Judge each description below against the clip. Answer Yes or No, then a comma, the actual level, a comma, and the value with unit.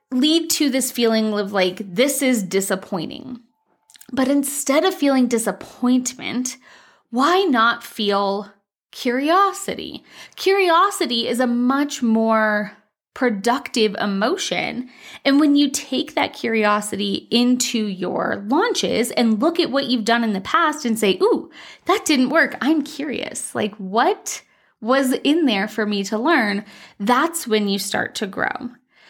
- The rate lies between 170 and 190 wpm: No, slow, 135 wpm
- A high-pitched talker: Yes, very high, 250 Hz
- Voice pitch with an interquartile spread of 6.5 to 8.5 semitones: No, average, 5.2 semitones